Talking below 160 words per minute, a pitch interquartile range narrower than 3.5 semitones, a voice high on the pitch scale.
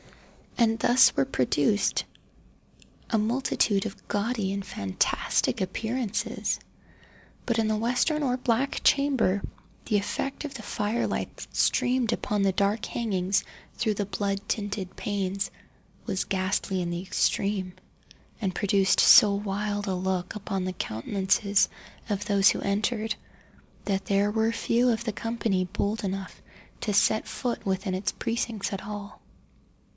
Yes: average, 140 wpm; average, 2.7 semitones; high, 205 Hz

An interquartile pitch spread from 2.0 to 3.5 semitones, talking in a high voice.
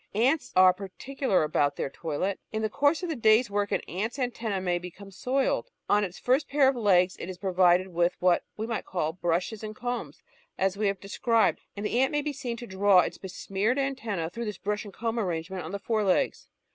No: average, 4.5 semitones; high, 205 Hz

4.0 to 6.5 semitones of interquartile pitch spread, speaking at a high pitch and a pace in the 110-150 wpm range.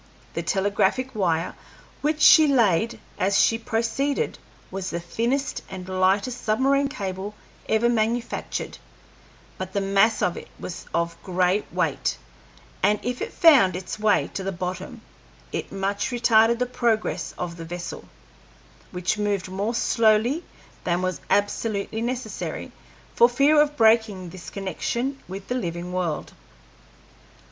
Yes: average, 4.3 semitones; high, 205 Hz; slow, 135 wpm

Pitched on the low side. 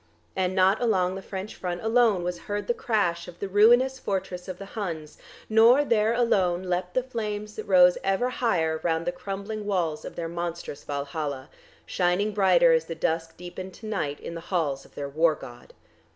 No: medium, 185 Hz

